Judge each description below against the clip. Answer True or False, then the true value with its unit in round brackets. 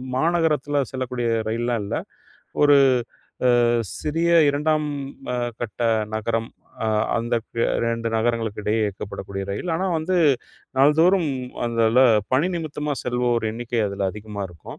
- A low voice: True (120 Hz)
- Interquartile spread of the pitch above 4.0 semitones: True (5.0 semitones)